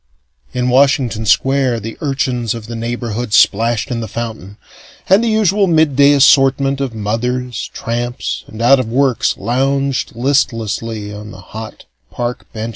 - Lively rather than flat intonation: No, average, 3.2 semitones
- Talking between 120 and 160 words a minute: Yes, average, 145 wpm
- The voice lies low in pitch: Yes, low, 120 Hz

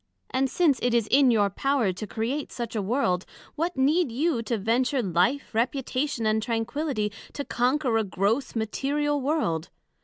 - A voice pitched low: No, high, 245 Hz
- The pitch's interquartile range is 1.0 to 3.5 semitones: No, average, 4.4 semitones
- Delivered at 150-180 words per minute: Yes, average, 160 wpm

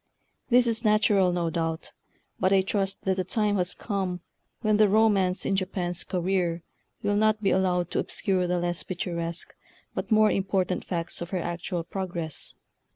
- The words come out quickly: No, average, 170 wpm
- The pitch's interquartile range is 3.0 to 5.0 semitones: No, narrow, 2.6 semitones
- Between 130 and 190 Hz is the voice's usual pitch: Yes, medium, 185 Hz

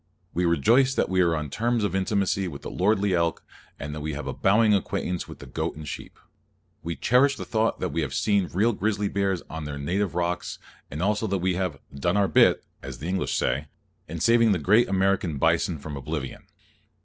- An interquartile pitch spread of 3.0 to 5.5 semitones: Yes, average, 4.7 semitones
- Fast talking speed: Yes, fast, 210 wpm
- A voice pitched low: Yes, very low, 90 Hz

